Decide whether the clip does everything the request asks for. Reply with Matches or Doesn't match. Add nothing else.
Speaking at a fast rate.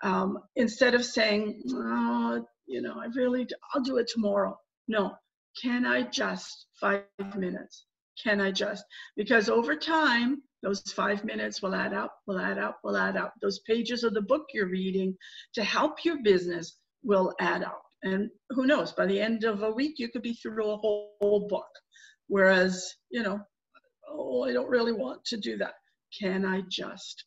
Doesn't match